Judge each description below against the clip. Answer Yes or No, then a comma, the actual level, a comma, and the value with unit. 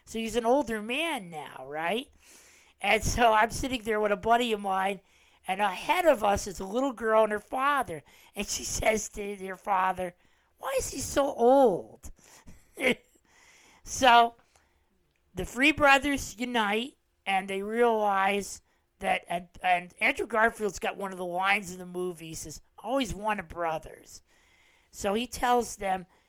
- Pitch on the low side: No, high, 210 Hz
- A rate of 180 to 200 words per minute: No, average, 160 wpm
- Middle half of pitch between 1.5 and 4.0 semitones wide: No, average, 4.4 semitones